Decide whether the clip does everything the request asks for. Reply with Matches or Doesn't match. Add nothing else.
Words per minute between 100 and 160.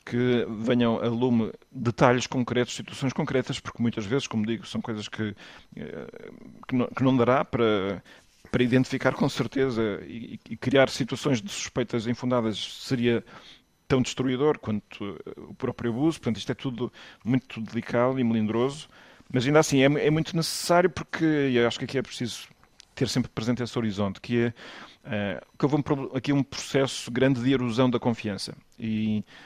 Doesn't match